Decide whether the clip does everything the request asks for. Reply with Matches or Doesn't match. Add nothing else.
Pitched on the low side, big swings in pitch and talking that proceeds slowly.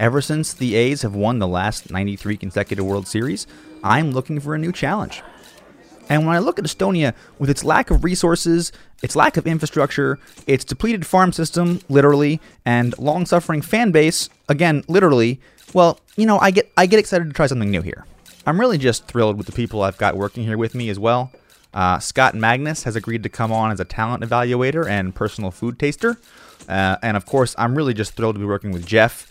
Doesn't match